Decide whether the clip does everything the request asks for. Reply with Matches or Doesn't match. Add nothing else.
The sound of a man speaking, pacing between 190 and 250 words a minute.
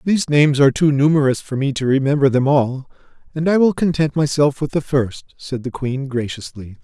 Matches